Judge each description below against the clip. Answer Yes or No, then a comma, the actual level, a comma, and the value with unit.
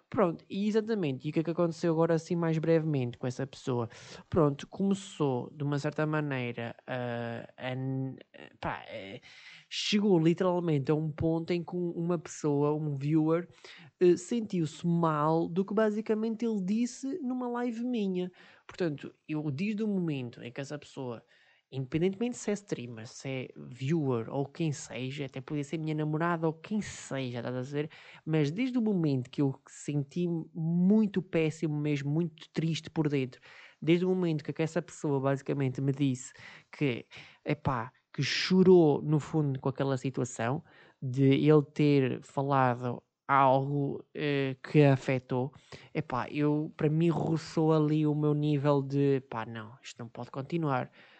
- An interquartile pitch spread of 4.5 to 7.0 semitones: No, average, 4.0 semitones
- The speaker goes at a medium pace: Yes, average, 155 wpm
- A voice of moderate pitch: Yes, medium, 150 Hz